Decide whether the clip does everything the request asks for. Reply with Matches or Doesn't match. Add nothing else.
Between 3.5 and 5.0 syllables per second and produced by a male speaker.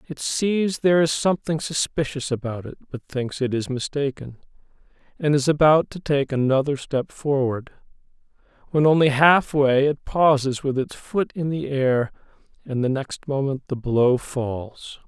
Matches